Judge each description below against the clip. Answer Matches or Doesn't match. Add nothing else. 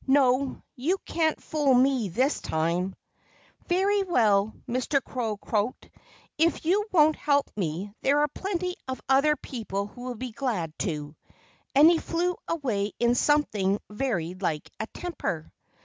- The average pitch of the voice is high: Matches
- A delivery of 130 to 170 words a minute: Matches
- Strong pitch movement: Matches